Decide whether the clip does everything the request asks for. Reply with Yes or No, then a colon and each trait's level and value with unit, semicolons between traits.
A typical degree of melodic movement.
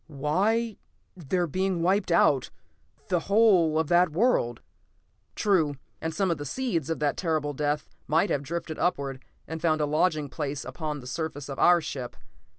Yes: average, 3.6 semitones